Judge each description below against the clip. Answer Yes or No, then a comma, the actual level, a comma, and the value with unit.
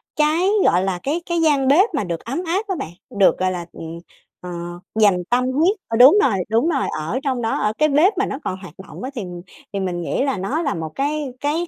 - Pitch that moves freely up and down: Yes, wide, 8.2 semitones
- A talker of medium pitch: No, very high, 265 Hz